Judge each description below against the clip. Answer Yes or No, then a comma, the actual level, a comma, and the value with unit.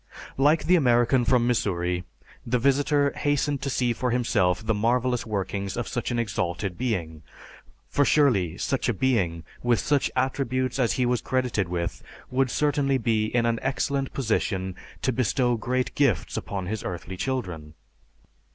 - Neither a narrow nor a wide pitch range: Yes, average, 4.9 semitones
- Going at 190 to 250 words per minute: No, average, 155 wpm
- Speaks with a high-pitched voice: No, low, 120 Hz